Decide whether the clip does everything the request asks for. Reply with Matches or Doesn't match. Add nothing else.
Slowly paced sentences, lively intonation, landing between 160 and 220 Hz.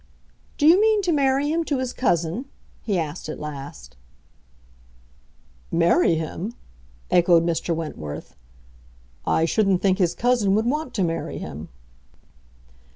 Matches